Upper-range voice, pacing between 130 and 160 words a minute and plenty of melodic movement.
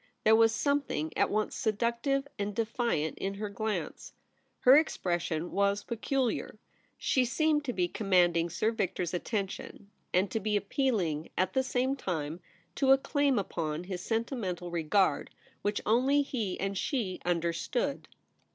Yes: high, 210 Hz; average, 145 wpm; wide, 5.7 semitones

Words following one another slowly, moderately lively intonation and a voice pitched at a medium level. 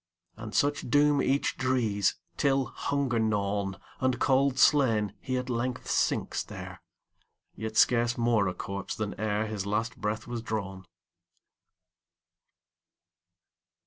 No: slow, 105 wpm; average, 3.7 semitones; low, 115 Hz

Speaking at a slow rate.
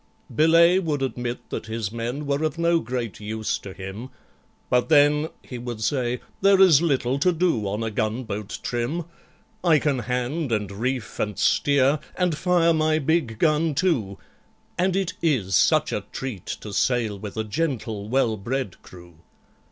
No: average, 165 wpm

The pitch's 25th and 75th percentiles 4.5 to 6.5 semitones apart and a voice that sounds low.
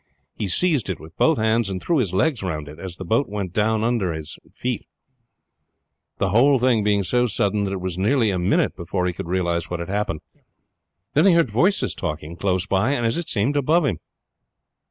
Yes: average, 5.3 semitones; low, 100 Hz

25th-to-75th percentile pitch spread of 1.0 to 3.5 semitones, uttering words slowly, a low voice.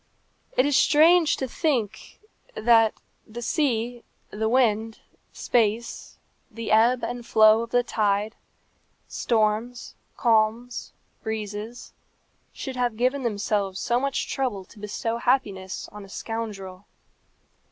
No: narrow, 2.5 semitones; slow, 115 wpm; high, 230 Hz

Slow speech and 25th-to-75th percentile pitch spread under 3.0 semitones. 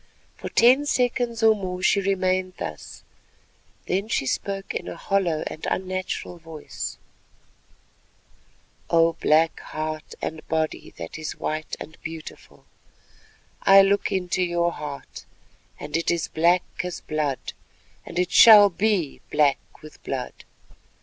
No: slow, 130 wpm; average, 3.8 semitones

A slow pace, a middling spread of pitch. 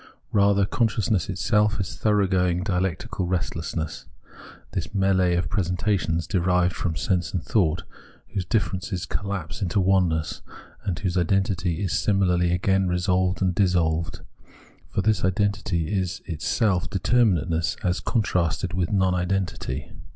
No: slow, 125 wpm; narrow, 2.2 semitones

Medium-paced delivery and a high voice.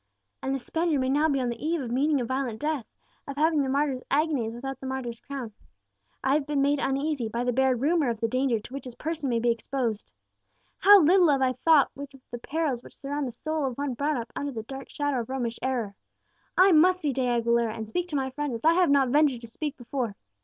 No: fast, 245 wpm; very high, 270 Hz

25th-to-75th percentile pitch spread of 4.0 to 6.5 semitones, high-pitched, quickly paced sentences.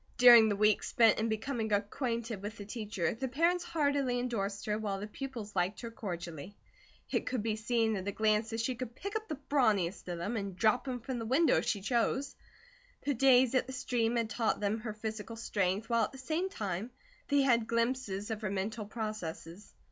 No: average, 3.4 semitones; high, 225 Hz; fast, 210 wpm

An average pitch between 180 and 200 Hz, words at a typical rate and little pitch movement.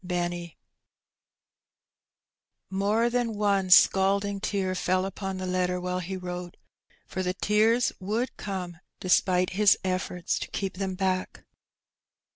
No: medium, 185 Hz; slow, 125 wpm; narrow, 1.6 semitones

